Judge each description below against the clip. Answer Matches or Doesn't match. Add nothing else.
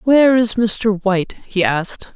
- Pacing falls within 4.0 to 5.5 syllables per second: Matches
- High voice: Matches